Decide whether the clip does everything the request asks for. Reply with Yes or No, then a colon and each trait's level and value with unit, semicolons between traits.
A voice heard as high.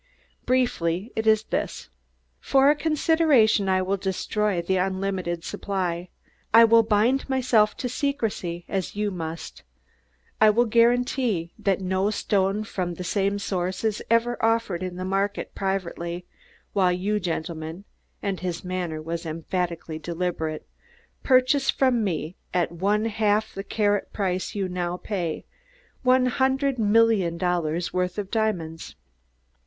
Yes: high, 195 Hz